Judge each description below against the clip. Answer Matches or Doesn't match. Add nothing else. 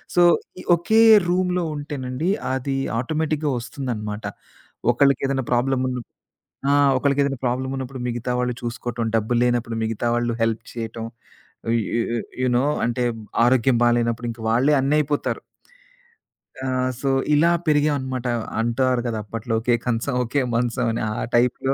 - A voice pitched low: Matches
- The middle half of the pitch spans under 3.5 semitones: Matches